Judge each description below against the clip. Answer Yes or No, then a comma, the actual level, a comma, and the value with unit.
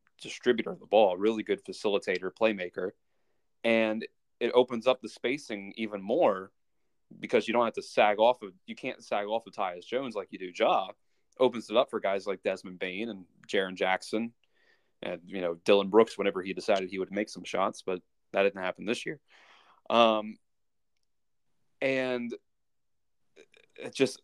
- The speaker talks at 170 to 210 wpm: Yes, average, 175 wpm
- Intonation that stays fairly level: No, average, 4.1 semitones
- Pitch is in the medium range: No, low, 110 Hz